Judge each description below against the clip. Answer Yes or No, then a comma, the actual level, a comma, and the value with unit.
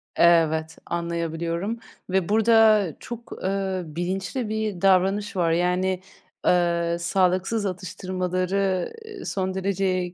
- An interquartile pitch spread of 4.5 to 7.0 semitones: No, narrow, 2.4 semitones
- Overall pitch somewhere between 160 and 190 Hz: Yes, medium, 185 Hz